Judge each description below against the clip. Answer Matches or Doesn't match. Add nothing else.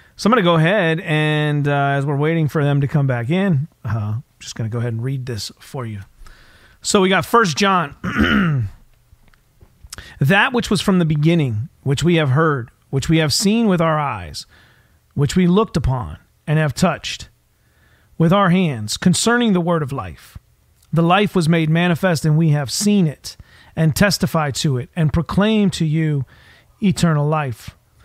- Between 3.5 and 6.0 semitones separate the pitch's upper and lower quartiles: Matches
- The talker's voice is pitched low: Doesn't match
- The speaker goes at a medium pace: Matches